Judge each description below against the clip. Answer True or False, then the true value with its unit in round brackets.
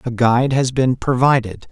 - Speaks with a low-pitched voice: True (125 Hz)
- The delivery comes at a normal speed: True (175 wpm)